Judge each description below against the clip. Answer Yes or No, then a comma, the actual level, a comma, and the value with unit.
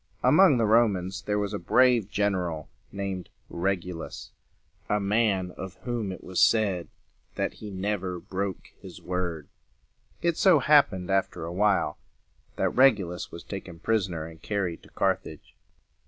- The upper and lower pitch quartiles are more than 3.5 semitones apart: No, average, 3.1 semitones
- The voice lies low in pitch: Yes, very low, 95 Hz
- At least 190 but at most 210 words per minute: No, average, 170 wpm